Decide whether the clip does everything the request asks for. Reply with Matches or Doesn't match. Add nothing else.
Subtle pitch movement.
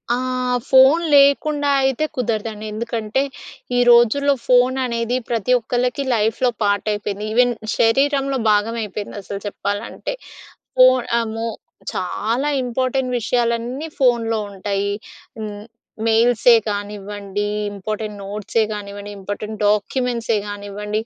Doesn't match